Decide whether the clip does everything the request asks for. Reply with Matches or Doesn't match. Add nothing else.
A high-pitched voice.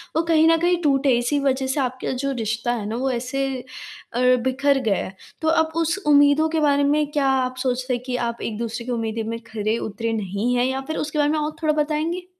Matches